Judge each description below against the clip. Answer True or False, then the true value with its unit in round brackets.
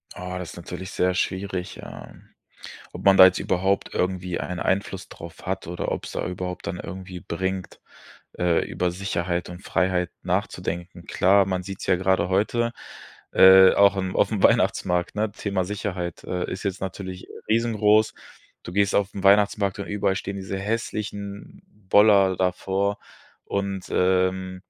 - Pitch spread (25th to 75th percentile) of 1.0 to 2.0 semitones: True (1.6 semitones)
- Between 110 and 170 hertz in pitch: False (95 Hz)